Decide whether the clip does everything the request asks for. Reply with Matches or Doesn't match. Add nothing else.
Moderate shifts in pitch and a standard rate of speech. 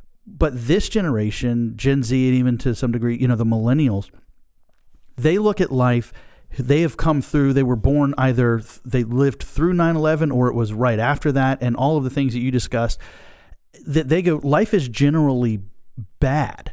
Matches